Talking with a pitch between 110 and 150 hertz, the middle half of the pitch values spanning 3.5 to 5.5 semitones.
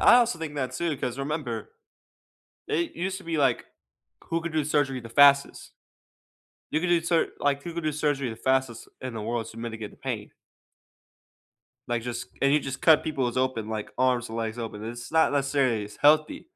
Yes: low, 135 Hz; average, 4.7 semitones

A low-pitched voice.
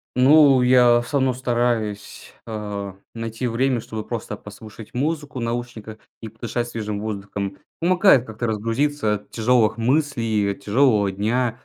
Yes: low, 115 Hz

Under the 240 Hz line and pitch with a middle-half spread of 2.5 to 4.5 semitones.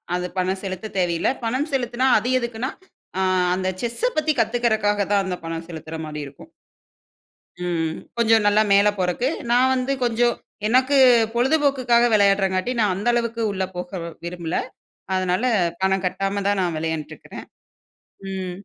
No: high, 200 Hz; average, 4.9 semitones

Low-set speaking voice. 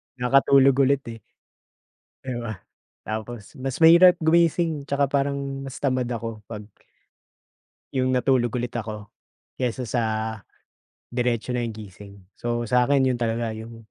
Yes: low, 125 Hz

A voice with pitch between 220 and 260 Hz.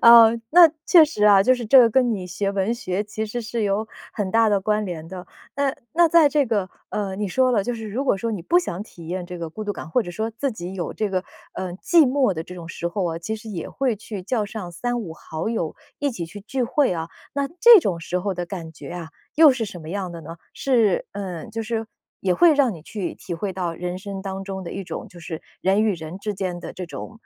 No: high, 205 Hz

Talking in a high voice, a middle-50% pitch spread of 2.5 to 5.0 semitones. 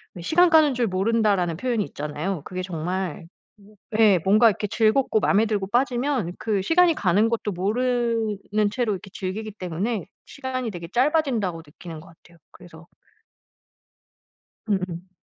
Yes: high, 210 Hz; average, 4.7 semitones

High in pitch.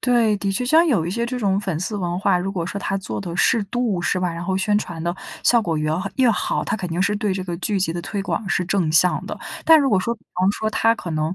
Yes: high, 195 Hz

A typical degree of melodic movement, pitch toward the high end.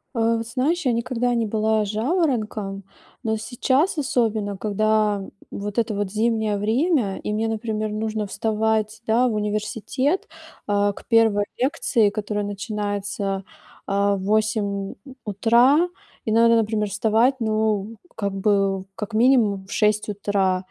No: narrow, 2.1 semitones; high, 215 Hz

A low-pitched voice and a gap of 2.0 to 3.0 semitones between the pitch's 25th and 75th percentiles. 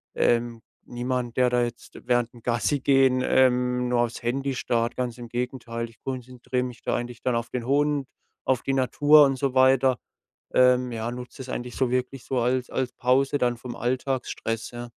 No: low, 125 Hz; narrow, 1.4 semitones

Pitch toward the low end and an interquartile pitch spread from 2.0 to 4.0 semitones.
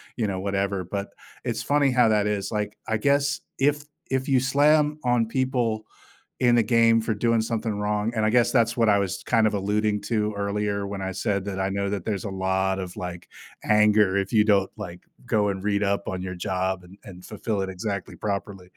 Yes: low, 105 Hz; average, 2.9 semitones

